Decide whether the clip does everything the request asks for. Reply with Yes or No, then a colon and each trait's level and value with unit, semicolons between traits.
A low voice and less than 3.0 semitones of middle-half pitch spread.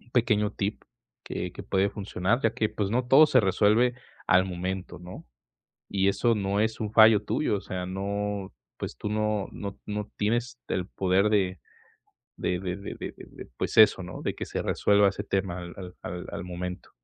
Yes: low, 100 Hz; narrow, 2.5 semitones